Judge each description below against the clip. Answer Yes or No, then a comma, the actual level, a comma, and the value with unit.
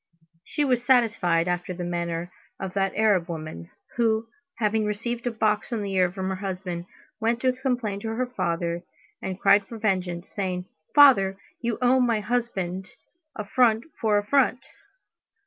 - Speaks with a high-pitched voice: Yes, high, 205 Hz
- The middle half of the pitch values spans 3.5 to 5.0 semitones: Yes, average, 4.6 semitones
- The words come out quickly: No, average, 155 wpm